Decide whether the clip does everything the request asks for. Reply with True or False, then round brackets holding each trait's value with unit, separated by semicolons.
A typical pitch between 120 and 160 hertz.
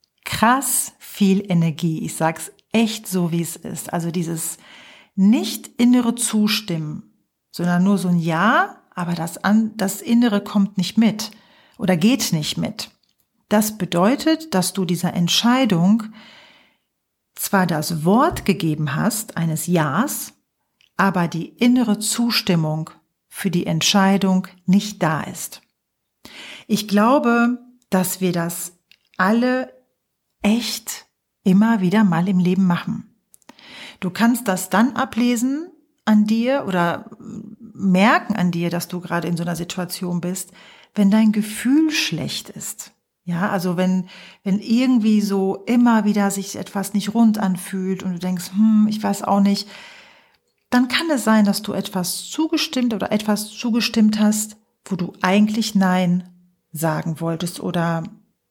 False (200 Hz)